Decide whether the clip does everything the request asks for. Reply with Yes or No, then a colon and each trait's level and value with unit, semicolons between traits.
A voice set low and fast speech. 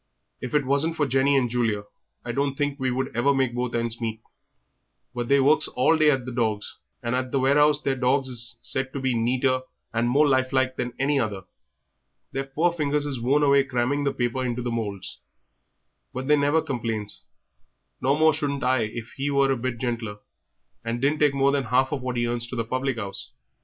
Yes: low, 130 Hz; fast, 210 wpm